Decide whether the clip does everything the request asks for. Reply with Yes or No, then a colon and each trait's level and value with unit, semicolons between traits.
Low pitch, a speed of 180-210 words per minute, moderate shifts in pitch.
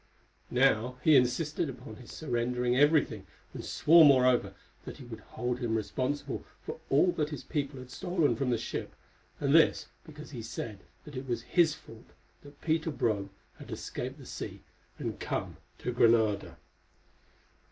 No: low, 130 Hz; average, 165 wpm; average, 3.8 semitones